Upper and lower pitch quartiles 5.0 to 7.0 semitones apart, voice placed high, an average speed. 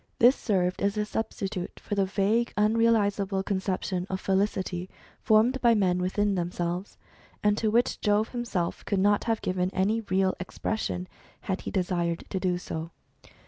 No: average, 2.7 semitones; high, 195 Hz; average, 155 wpm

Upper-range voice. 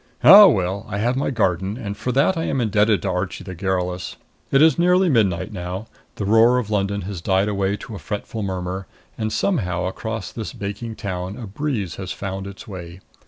No: low, 100 Hz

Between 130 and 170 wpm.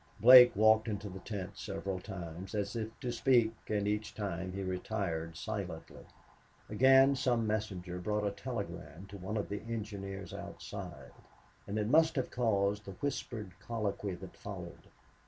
Yes: average, 155 wpm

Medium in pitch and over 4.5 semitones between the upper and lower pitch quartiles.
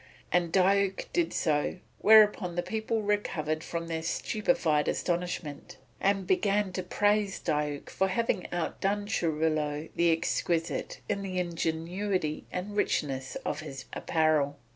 No: medium, 175 Hz; average, 4.1 semitones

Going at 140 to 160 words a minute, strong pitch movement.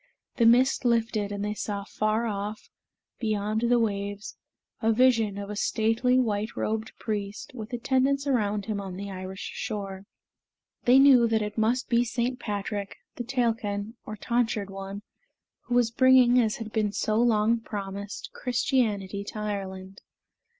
No: average, 150 wpm; average, 2.8 semitones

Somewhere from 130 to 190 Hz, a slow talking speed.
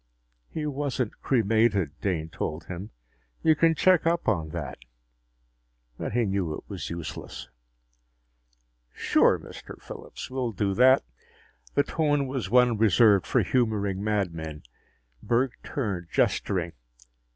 No: low, 110 Hz; slow, 120 wpm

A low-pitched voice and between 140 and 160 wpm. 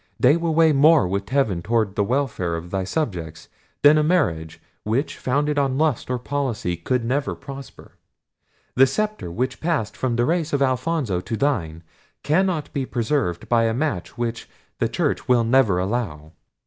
No: low, 125 Hz; average, 170 wpm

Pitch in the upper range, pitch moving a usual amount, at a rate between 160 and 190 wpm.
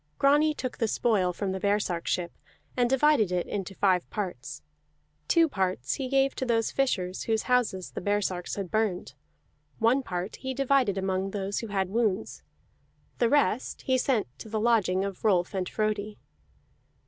Yes: high, 210 Hz; average, 4.9 semitones; average, 165 wpm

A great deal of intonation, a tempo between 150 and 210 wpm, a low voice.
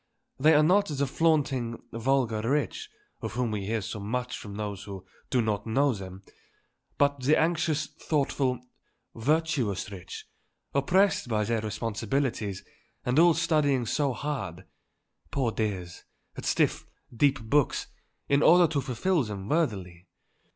No: wide, 5.7 semitones; slow, 135 wpm; low, 125 Hz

